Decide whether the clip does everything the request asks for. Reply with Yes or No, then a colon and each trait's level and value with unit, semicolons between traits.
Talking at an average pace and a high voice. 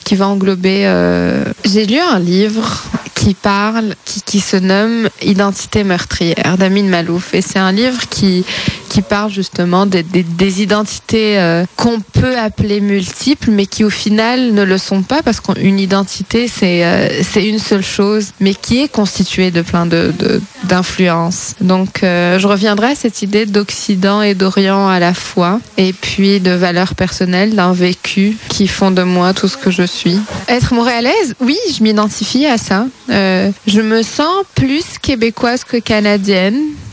Yes: average, 170 wpm; high, 200 Hz